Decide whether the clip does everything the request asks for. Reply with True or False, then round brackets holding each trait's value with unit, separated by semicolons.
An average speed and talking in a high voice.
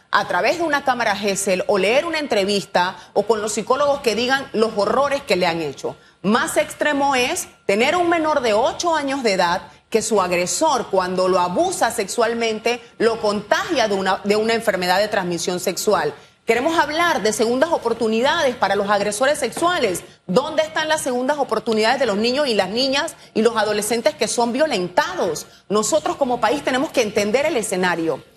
True (180 wpm; 230 Hz)